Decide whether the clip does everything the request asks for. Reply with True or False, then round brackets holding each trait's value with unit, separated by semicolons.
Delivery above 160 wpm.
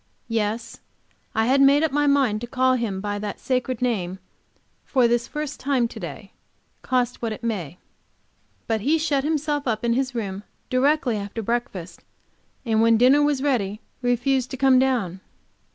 True (170 wpm)